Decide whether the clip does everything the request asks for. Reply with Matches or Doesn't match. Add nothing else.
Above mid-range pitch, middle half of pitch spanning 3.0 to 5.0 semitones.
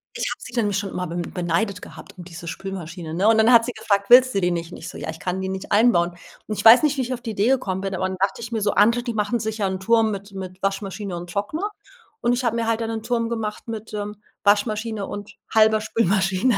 Matches